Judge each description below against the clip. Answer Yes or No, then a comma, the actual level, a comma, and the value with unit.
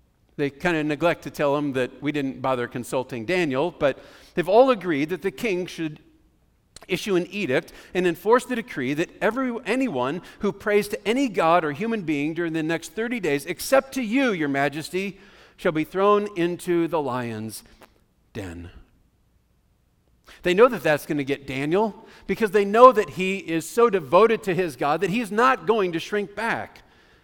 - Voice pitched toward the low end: No, medium, 180 Hz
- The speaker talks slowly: No, average, 180 wpm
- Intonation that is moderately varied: No, wide, 6.3 semitones